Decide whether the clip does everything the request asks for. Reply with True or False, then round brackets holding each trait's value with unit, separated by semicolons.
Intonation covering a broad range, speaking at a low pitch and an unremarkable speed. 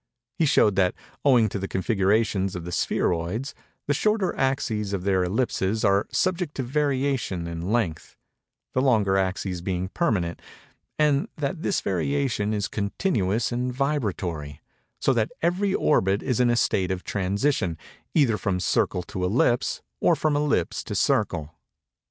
True (6.6 semitones; 105 Hz; 145 wpm)